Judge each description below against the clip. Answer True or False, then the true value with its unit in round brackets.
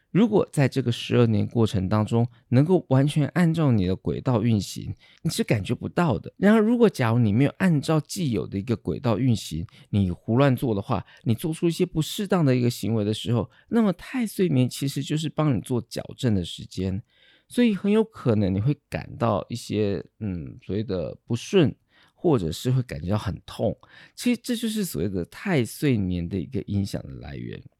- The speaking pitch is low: True (125 Hz)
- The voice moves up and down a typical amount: False (6.6 semitones)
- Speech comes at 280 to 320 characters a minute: True (295 characters per minute)